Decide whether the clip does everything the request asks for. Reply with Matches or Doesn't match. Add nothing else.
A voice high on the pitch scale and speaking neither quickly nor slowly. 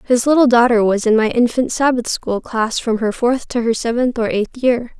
Doesn't match